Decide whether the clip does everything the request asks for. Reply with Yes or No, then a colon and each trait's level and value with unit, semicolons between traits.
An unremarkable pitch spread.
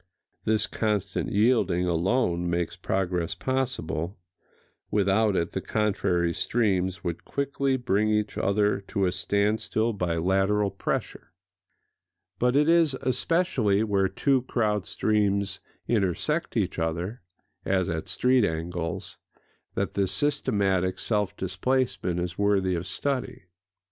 Yes: average, 3.9 semitones